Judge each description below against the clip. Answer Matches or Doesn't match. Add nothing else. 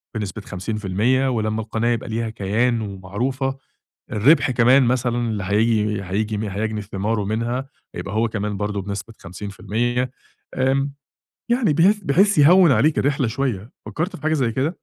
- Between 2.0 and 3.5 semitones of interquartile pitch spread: Doesn't match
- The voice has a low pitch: Matches